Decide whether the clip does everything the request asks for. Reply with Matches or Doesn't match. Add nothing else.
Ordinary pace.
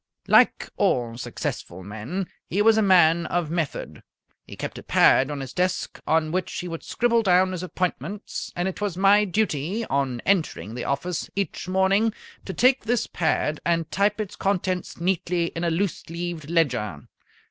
Matches